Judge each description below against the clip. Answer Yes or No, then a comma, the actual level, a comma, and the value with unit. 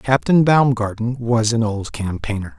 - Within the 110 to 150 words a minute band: Yes, average, 140 wpm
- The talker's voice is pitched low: Yes, low, 120 Hz